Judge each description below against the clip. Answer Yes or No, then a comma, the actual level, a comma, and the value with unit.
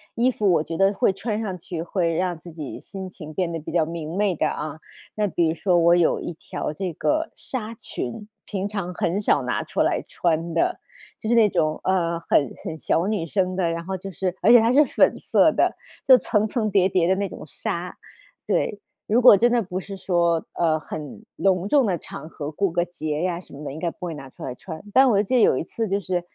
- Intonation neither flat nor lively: Yes, average, 3.6 semitones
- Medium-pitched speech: Yes, medium, 180 Hz